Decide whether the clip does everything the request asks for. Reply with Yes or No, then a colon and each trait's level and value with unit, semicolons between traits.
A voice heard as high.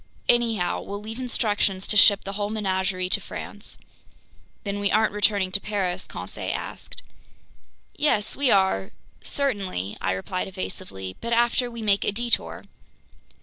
Yes: high, 205 Hz